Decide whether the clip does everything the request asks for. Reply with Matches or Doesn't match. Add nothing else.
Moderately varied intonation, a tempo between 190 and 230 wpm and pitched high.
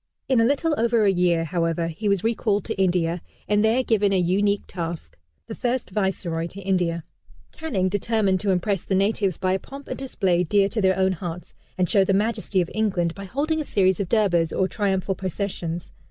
Matches